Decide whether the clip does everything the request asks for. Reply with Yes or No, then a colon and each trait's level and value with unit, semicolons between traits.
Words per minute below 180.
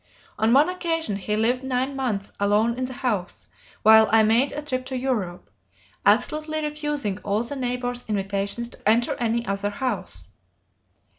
Yes: average, 155 wpm